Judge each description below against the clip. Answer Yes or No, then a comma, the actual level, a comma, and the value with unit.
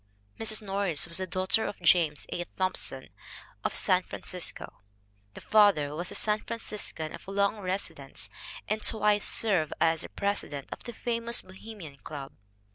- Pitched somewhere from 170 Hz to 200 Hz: Yes, high, 190 Hz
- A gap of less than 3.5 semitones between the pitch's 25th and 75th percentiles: No, average, 4.1 semitones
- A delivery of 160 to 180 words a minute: No, average, 150 wpm